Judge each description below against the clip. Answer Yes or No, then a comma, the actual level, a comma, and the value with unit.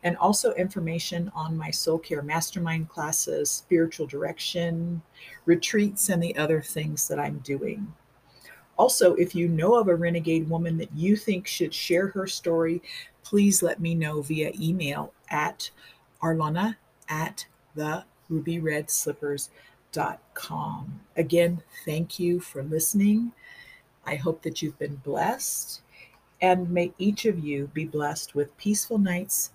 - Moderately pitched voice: Yes, medium, 165 Hz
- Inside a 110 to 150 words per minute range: Yes, average, 140 wpm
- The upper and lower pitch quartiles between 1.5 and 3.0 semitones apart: Yes, average, 2.7 semitones